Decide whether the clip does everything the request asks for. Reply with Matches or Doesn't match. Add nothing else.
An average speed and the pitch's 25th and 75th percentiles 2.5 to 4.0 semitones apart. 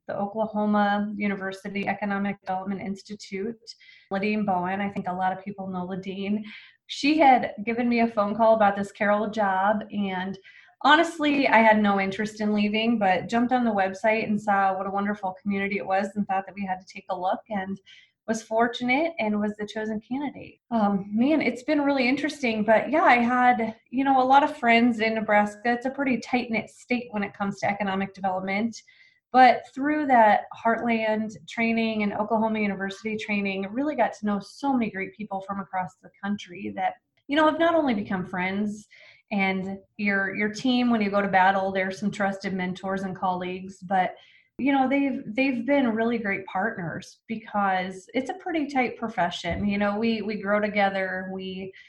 Matches